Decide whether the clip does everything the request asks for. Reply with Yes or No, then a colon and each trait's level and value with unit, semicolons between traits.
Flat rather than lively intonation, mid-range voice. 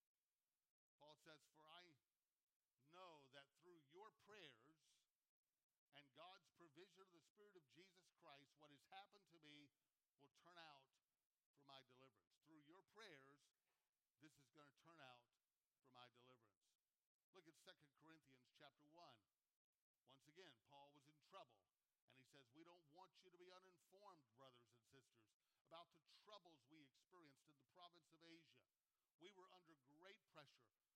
No: average, 4.3 semitones; medium, 150 Hz